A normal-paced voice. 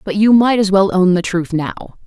No: fast, 260 wpm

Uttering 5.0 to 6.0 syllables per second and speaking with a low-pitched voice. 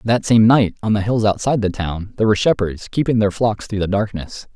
Yes: 5.9 syllables/s; low, 105 Hz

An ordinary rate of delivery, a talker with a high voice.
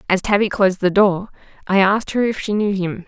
No: fast, 235 wpm; high, 195 Hz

